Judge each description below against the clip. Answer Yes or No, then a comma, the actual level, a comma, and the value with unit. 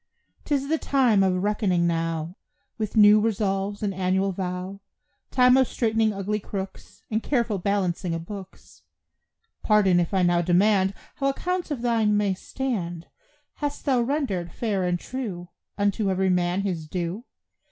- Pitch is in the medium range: No, high, 200 Hz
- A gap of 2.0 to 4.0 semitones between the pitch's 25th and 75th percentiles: Yes, average, 3.7 semitones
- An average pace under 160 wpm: Yes, average, 150 wpm